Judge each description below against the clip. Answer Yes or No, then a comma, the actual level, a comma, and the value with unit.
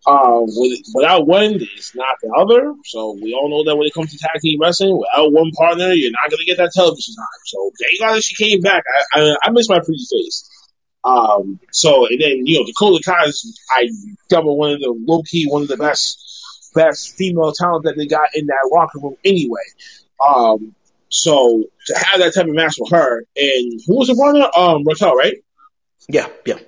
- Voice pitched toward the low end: No, medium, 170 Hz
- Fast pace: Yes, fast, 210 wpm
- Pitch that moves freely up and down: Yes, wide, 7.0 semitones